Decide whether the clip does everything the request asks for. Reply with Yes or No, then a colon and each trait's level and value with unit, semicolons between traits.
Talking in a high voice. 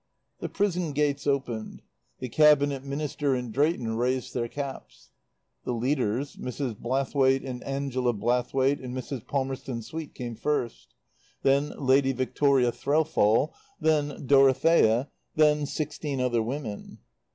No: low, 135 Hz